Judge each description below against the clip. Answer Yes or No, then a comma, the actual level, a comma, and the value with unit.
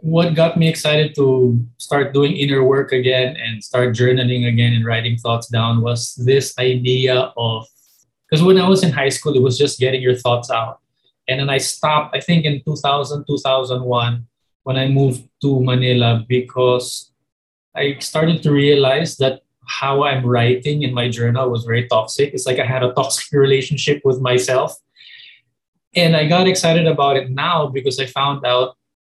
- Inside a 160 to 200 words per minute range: Yes, average, 175 wpm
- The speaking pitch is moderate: No, low, 130 Hz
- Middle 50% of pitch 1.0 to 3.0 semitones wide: Yes, narrow, 2.5 semitones